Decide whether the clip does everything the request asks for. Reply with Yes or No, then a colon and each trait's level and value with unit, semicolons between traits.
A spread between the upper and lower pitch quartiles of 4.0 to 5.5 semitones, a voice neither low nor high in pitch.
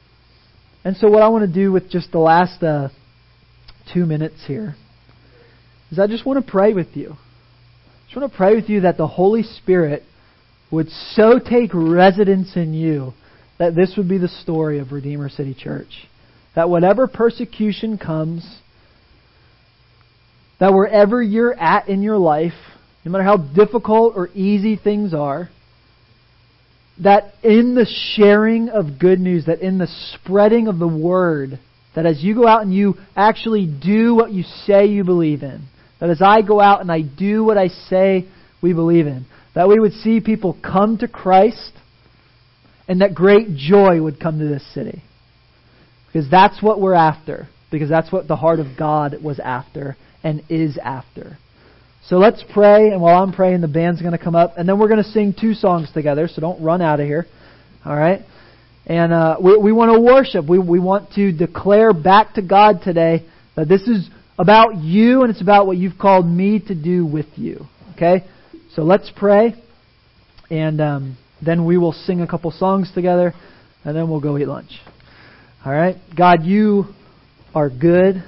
Yes: average, 5.0 semitones; medium, 175 Hz